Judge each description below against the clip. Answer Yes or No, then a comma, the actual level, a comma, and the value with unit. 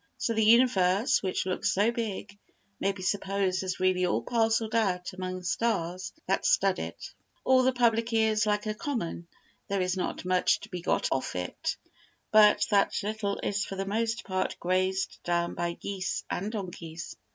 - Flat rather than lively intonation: No, average, 3.3 semitones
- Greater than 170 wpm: Yes, average, 180 wpm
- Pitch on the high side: Yes, high, 195 Hz